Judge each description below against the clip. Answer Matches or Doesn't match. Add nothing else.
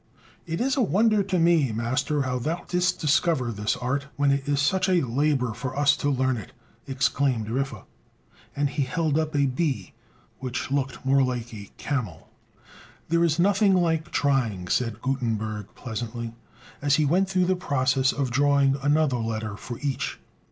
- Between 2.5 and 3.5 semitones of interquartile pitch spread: Doesn't match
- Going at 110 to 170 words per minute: Matches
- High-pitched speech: Doesn't match